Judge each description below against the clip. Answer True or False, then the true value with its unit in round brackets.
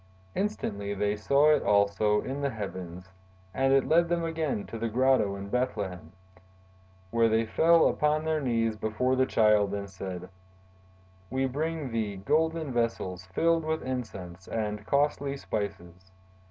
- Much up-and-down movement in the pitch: True (5.9 semitones)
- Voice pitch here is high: False (115 Hz)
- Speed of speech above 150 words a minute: False (145 wpm)